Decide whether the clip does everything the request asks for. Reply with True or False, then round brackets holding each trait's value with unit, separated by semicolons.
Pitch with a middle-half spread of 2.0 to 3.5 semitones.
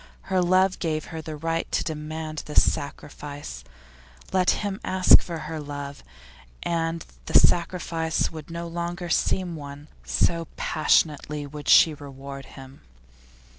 True (2.7 semitones)